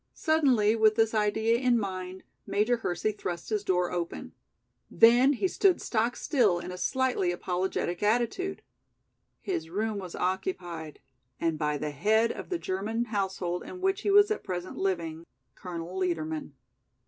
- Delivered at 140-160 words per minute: Yes, average, 150 wpm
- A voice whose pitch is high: Yes, high, 200 Hz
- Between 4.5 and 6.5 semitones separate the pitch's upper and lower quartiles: Yes, average, 5.0 semitones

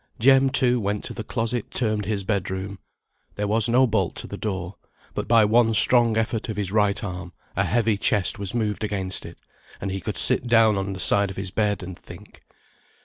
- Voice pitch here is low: Yes, low, 105 Hz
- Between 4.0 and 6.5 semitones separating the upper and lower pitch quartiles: No, average, 2.7 semitones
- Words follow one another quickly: Yes, fast, 210 wpm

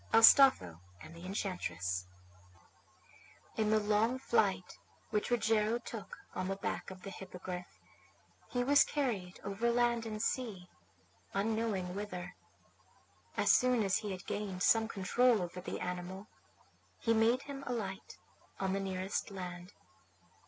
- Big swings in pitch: No, average, 3.8 semitones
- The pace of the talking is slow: Yes, slow, 130 wpm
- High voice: Yes, high, 200 Hz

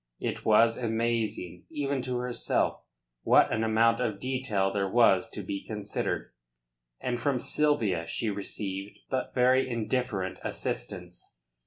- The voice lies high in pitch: No, low, 115 Hz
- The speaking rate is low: Yes, slow, 130 wpm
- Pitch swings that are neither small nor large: Yes, average, 4.1 semitones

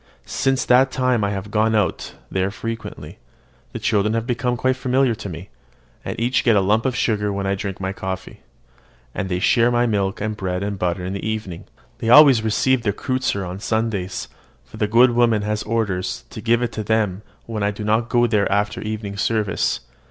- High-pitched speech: No, low, 110 Hz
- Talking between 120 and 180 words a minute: No, fast, 205 wpm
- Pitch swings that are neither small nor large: Yes, average, 3.1 semitones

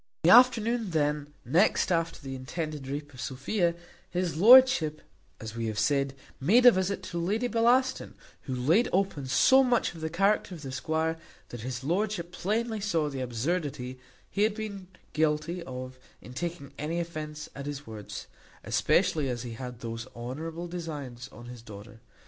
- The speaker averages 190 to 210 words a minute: No, average, 170 wpm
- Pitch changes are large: Yes, wide, 6.4 semitones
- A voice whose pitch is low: No, medium, 155 Hz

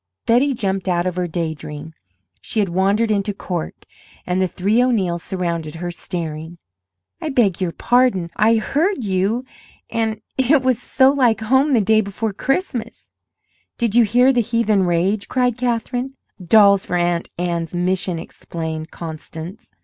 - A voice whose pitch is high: Yes, high, 200 Hz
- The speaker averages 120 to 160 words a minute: Yes, average, 155 wpm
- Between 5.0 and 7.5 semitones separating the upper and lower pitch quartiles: Yes, wide, 5.4 semitones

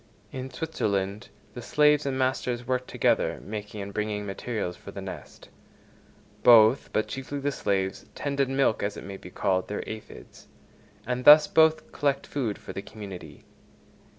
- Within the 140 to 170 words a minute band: Yes, average, 160 wpm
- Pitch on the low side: Yes, low, 120 Hz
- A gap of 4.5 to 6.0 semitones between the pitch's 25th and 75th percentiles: Yes, average, 5.1 semitones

